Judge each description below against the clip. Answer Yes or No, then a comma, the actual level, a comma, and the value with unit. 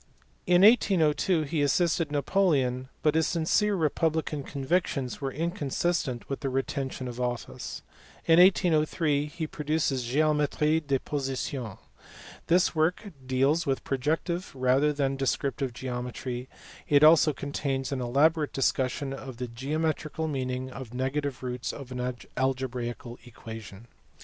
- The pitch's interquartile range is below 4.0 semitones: Yes, average, 3.5 semitones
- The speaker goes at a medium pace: No, slow, 130 wpm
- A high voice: No, medium, 140 Hz